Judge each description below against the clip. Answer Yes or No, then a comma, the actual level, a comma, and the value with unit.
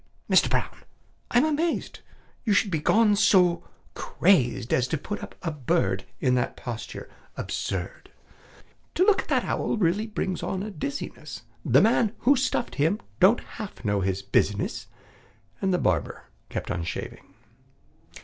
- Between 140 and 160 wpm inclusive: Yes, average, 150 wpm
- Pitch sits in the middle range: Yes, medium, 180 Hz